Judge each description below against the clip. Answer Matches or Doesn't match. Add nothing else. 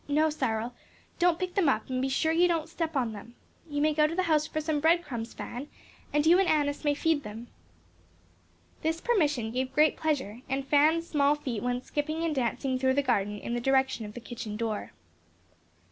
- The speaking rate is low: Doesn't match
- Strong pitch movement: Doesn't match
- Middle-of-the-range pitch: Doesn't match